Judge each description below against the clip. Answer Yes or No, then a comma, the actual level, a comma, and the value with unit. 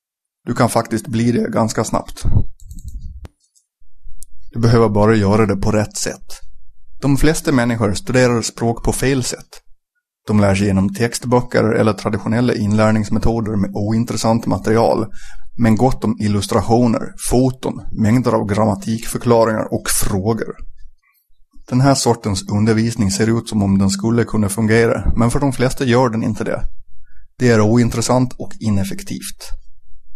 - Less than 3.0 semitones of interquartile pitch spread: Yes, narrow, 2.5 semitones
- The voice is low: Yes, low, 110 Hz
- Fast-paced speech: No, average, 135 wpm